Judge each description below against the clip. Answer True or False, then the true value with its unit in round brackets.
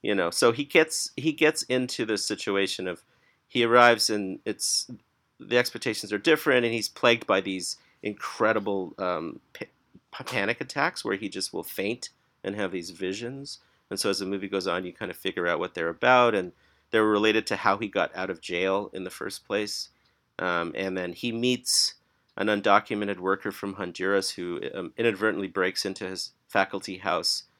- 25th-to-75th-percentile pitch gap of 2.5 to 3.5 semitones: False (3.9 semitones)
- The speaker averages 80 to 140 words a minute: False (185 wpm)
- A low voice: True (105 Hz)